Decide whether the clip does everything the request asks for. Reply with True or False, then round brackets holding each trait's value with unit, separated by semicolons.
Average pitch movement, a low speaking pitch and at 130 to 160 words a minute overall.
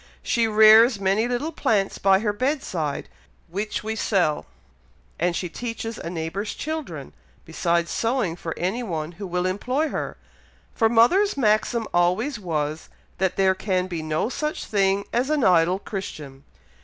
False (4.9 semitones; 195 Hz; 150 wpm)